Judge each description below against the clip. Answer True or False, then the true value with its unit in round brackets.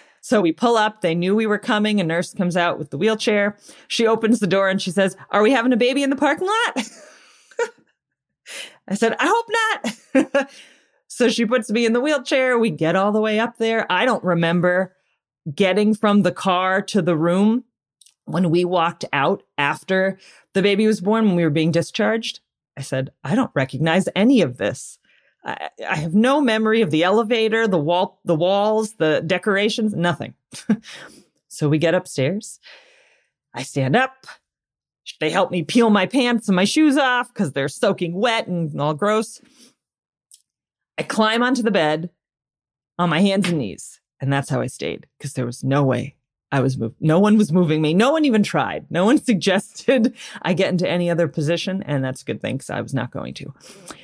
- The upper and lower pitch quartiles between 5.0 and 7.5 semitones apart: True (5.3 semitones)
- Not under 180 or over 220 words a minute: True (190 wpm)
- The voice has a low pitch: False (195 Hz)